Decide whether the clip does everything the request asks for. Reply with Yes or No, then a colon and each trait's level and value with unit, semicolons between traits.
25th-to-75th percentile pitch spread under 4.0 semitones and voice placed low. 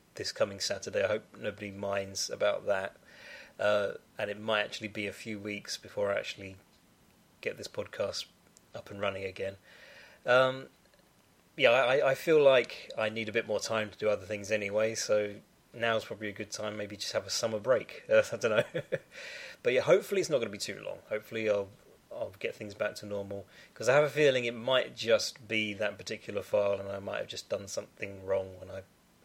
Yes: narrow, 2.4 semitones; low, 105 Hz